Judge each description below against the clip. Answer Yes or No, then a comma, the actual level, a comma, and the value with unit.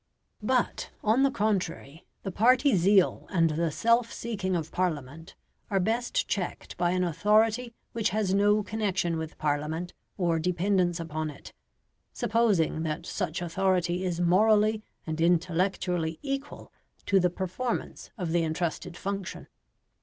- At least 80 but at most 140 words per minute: Yes, slow, 135 wpm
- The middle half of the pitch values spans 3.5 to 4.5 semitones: Yes, average, 4.1 semitones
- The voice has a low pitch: No, medium, 185 Hz